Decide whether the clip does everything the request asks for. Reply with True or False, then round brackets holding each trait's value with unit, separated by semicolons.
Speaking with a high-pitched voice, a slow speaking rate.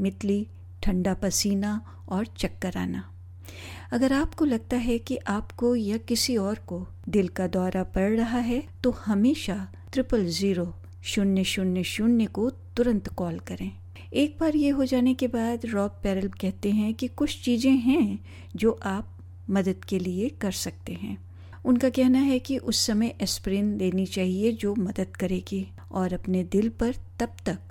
False (200 Hz; 160 wpm)